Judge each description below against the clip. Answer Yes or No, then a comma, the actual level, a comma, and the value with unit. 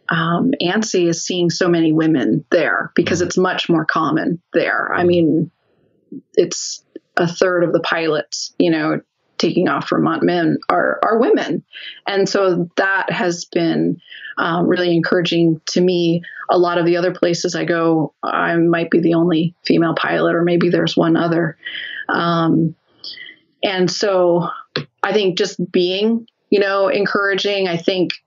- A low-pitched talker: No, medium, 175 Hz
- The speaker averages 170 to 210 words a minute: No, average, 155 wpm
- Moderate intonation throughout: No, narrow, 1.7 semitones